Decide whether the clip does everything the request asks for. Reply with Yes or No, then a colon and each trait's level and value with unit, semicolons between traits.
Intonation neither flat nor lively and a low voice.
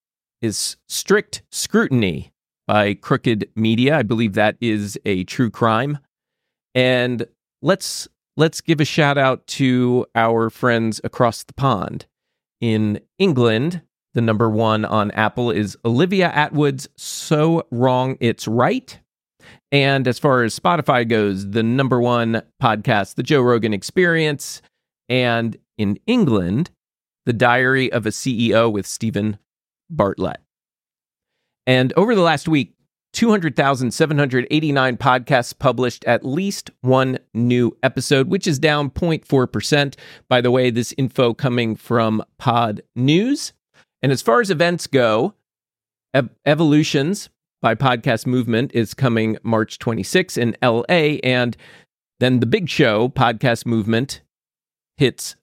Yes: average, 3.9 semitones; low, 125 Hz